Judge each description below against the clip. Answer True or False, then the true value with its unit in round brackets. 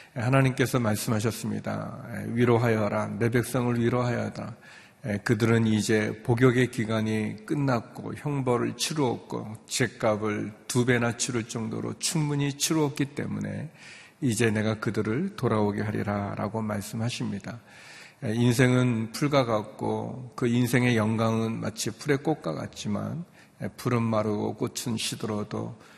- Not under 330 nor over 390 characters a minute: False (285 characters per minute)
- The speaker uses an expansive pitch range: False (2.7 semitones)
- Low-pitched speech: True (115 Hz)